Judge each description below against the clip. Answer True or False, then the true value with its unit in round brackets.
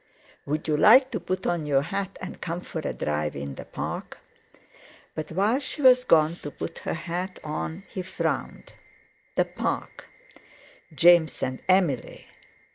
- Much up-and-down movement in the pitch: False (3.8 semitones)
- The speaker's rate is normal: True (155 wpm)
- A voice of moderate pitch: True (170 Hz)